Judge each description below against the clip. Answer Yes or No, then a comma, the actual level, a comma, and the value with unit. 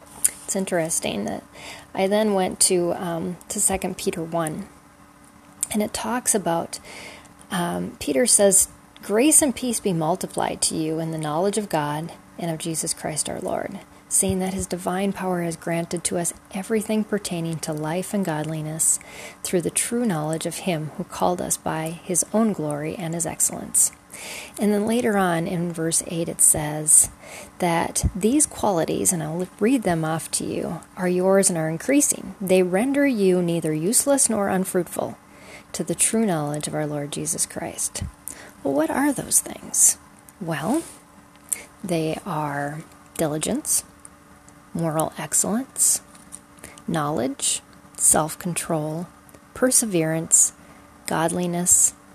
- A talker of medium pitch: Yes, medium, 175 Hz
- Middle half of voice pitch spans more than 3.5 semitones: Yes, average, 4.0 semitones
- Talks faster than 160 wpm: No, average, 145 wpm